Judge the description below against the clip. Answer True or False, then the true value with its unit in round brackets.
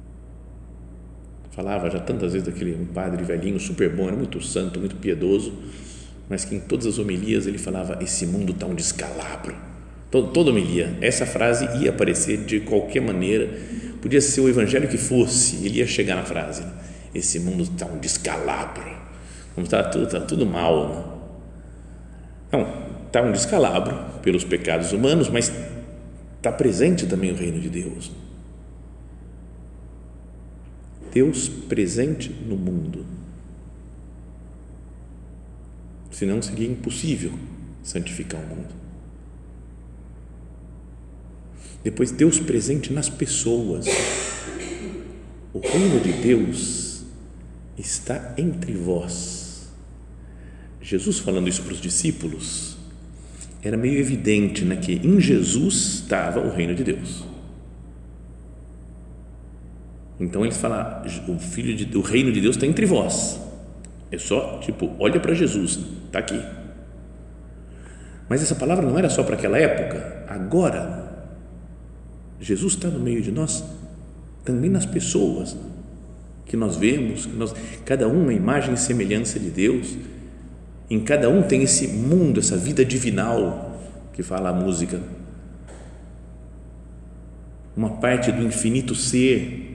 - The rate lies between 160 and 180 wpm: False (125 wpm)